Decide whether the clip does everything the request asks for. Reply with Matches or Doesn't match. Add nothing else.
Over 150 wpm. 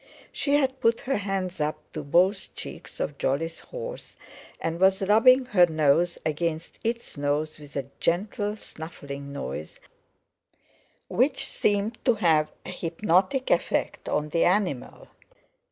Doesn't match